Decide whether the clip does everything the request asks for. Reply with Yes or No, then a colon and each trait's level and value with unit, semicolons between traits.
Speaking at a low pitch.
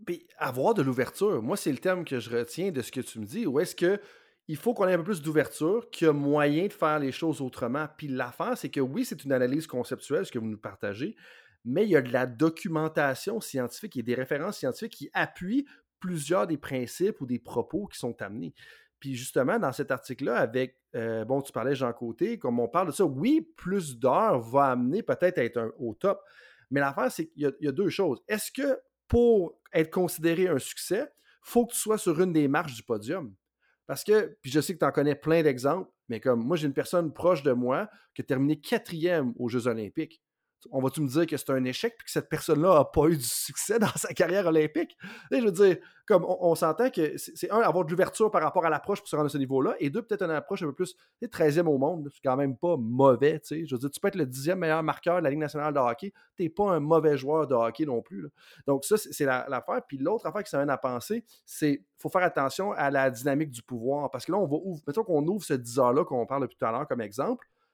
No: medium, 155 Hz